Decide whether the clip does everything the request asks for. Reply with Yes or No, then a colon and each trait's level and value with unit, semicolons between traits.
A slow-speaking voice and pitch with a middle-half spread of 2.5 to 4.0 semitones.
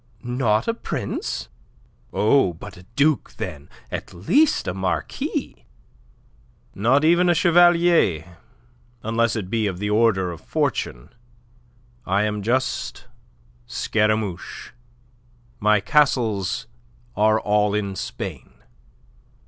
No: slow, 105 wpm; average, 5.2 semitones